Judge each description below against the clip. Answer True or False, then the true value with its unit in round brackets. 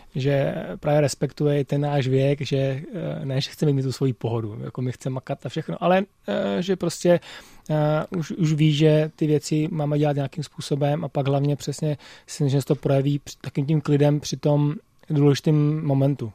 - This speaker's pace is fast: True (180 wpm)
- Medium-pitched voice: True (145 Hz)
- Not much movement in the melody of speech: True (1.9 semitones)